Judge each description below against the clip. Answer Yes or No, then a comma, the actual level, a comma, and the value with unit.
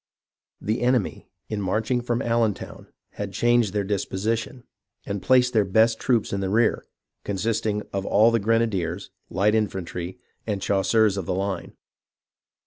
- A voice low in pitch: Yes, low, 105 Hz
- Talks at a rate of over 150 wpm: No, average, 140 wpm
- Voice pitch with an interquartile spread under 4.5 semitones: Yes, average, 2.9 semitones